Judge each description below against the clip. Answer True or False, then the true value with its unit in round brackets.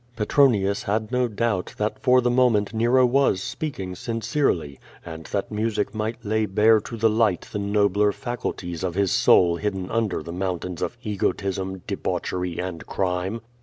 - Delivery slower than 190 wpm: True (165 wpm)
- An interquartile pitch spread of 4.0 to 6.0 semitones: False (3.6 semitones)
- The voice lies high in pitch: False (105 Hz)